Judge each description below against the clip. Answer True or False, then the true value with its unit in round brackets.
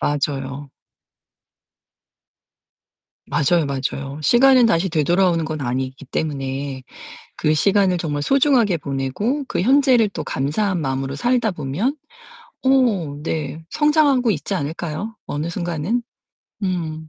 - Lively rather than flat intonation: True (7.6 semitones)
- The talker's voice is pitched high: False (165 Hz)